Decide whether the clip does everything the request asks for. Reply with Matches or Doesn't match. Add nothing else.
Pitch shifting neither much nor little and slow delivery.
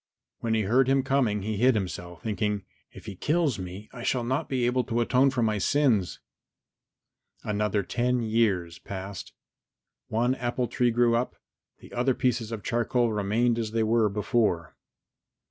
Doesn't match